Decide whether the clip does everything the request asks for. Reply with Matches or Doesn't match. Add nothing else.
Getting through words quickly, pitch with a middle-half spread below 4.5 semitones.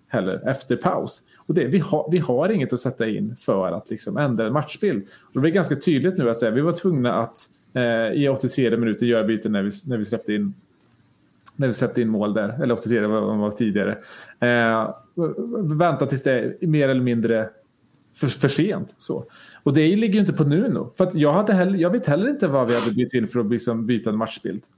Doesn't match